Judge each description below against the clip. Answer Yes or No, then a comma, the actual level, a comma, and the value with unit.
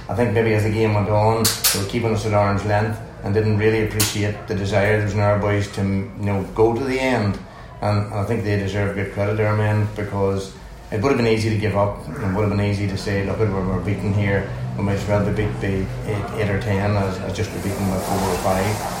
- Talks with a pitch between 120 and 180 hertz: No, low, 105 Hz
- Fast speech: Yes, fast, 255 wpm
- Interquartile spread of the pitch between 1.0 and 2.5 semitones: Yes, narrow, 1.5 semitones